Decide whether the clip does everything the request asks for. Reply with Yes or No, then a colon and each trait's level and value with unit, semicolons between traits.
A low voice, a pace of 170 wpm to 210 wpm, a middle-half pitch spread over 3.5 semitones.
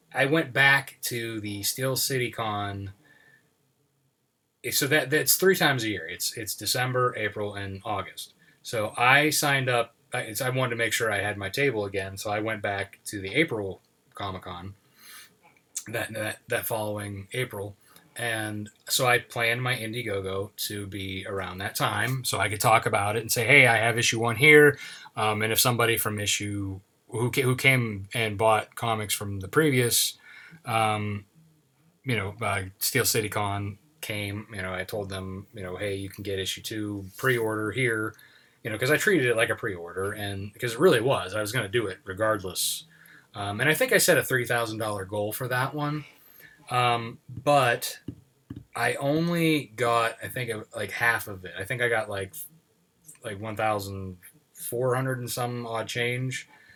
Yes: low, 115 Hz; average, 185 wpm; average, 4.1 semitones